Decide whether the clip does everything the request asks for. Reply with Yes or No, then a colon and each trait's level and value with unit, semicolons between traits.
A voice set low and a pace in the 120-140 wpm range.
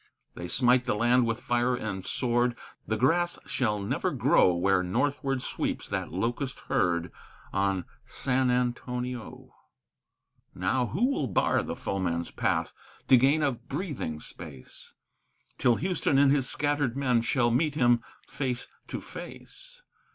Yes: low, 125 Hz; slow, 135 wpm